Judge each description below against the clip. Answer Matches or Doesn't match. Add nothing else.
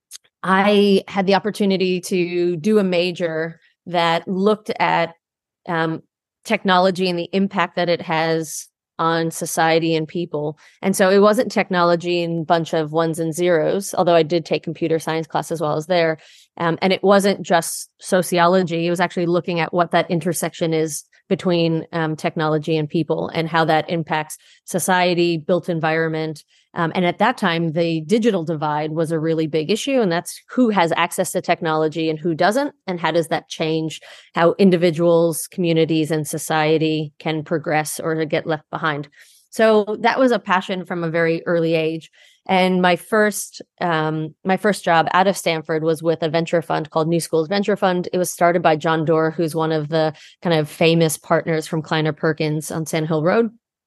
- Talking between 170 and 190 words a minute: Matches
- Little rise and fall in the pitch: Matches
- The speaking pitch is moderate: Matches